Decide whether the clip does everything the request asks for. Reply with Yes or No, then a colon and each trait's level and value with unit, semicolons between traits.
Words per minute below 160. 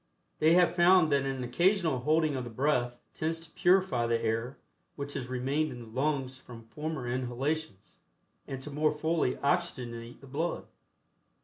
No: average, 165 wpm